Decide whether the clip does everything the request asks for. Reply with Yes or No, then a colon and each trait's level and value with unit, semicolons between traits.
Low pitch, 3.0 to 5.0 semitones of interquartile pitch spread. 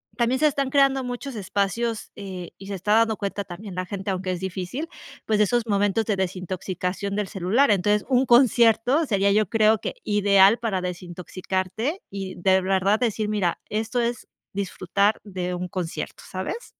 No: high, 200 Hz; average, 3.4 semitones